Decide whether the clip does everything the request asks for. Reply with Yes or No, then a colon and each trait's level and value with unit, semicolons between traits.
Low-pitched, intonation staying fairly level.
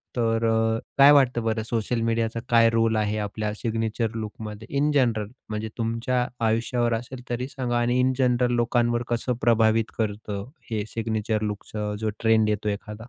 Yes: low, 115 Hz; narrow, 1.6 semitones